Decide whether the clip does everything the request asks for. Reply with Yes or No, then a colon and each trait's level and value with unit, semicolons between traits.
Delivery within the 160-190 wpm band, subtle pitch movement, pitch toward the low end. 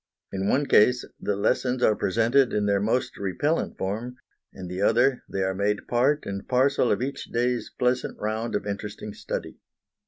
No: average, 180 wpm; average, 3.8 semitones; low, 115 Hz